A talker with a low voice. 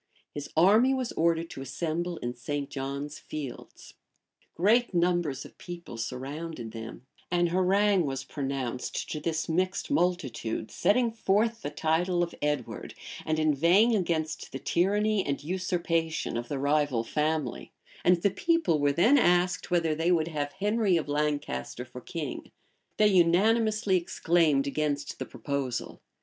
No: medium, 165 Hz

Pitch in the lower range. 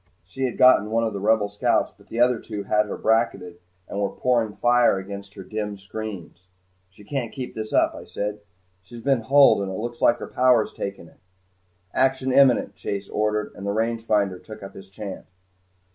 Yes: low, 110 Hz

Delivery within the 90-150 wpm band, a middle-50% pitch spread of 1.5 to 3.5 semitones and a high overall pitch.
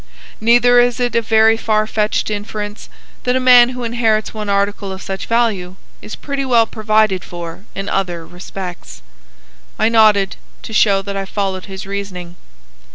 No: average, 160 wpm; average, 2.9 semitones; high, 210 Hz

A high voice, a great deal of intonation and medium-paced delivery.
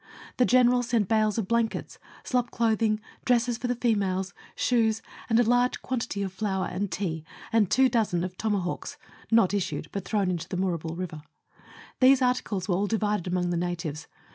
No: high, 210 Hz; average, 4.3 semitones; average, 175 wpm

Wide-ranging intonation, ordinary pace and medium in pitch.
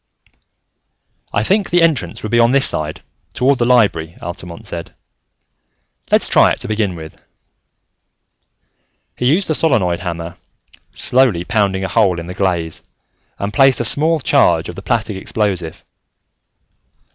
No: wide, 6.3 semitones; average, 145 wpm; low, 105 Hz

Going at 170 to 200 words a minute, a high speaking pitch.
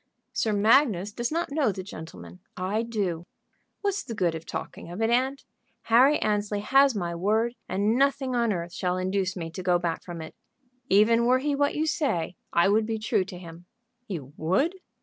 Yes: average, 190 wpm; high, 210 Hz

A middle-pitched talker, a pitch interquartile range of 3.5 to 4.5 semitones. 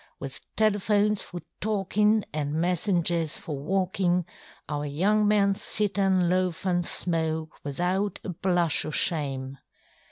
Yes: medium, 180 Hz; average, 3.9 semitones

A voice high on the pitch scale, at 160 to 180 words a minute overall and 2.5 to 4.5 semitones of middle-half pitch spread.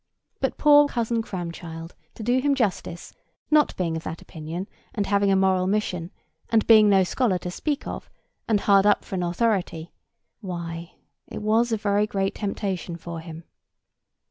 Yes: high, 195 Hz; average, 165 wpm; average, 4.2 semitones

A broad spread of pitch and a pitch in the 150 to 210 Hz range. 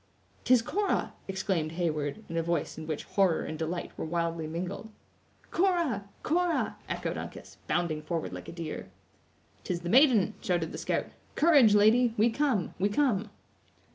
Yes: wide, 6.2 semitones; high, 190 Hz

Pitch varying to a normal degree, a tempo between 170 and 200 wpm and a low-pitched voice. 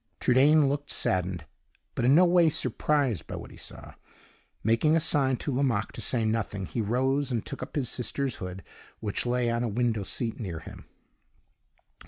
Yes: average, 4.3 semitones; average, 180 wpm; low, 125 Hz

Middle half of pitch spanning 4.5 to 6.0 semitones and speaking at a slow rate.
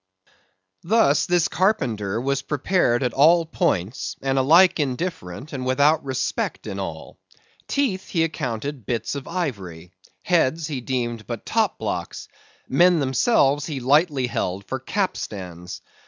Yes: wide, 5.5 semitones; slow, 130 wpm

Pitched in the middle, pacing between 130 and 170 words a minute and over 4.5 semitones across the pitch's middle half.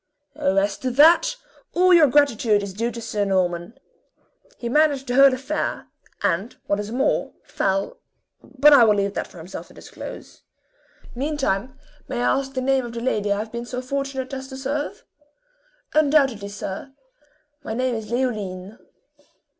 No: high, 245 Hz; average, 165 wpm; average, 4.9 semitones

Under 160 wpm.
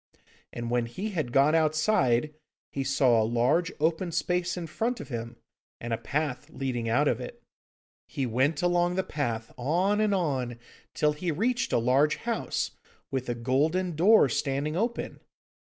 No: average, 165 wpm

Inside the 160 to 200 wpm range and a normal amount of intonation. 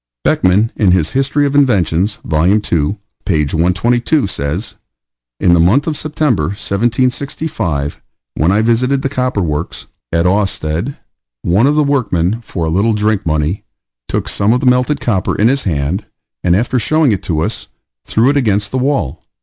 No: average, 165 wpm; wide, 6.7 semitones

